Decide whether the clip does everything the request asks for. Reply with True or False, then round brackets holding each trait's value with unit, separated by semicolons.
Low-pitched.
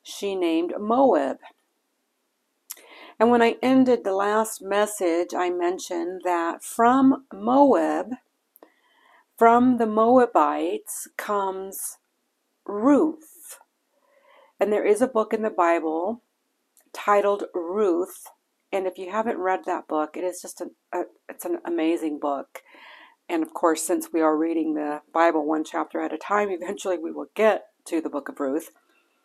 False (200 Hz)